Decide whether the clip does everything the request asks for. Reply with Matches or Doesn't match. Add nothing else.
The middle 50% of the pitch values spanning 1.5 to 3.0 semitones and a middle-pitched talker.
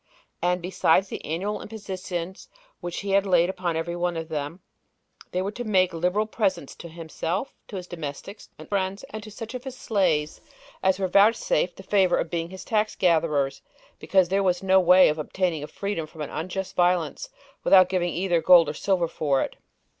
Matches